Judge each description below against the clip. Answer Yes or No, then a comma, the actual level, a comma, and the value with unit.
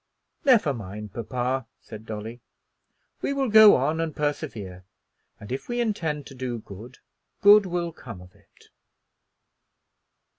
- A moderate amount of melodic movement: No, wide, 7.7 semitones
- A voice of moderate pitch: No, low, 130 Hz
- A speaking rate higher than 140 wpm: No, slow, 135 wpm